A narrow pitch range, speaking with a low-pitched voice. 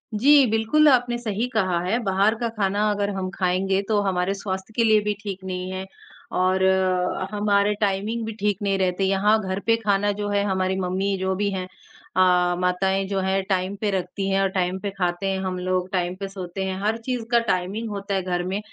No: narrow, 1.9 semitones; high, 195 Hz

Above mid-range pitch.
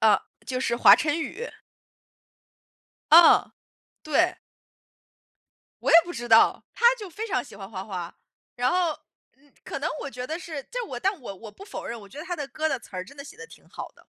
Yes: very high, 285 Hz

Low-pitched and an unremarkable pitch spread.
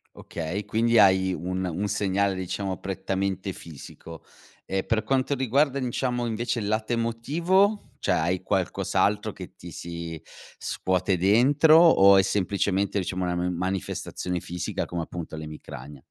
Yes: very low, 95 Hz; average, 4.4 semitones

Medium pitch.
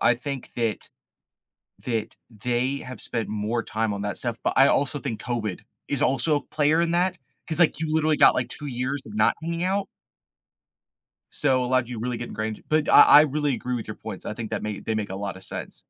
No: low, 125 Hz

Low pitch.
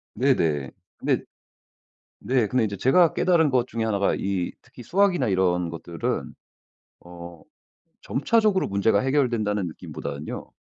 Yes: low, 110 Hz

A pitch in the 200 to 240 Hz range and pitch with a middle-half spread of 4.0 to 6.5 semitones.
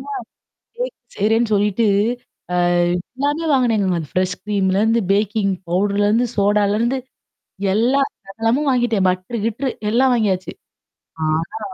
No: high, 215 Hz; average, 3.5 semitones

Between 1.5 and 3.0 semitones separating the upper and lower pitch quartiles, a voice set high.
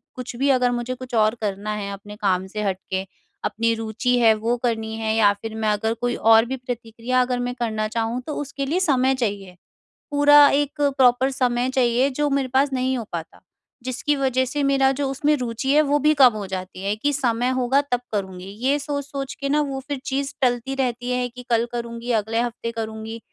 No: average, 3.4 semitones; high, 245 Hz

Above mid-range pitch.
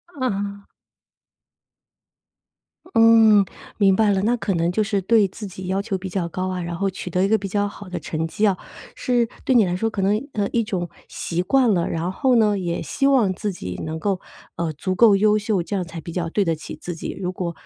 Yes: high, 195 Hz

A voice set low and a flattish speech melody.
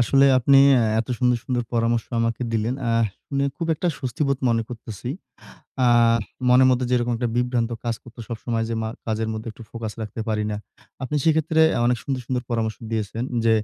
Yes: low, 120 Hz; narrow, 2.1 semitones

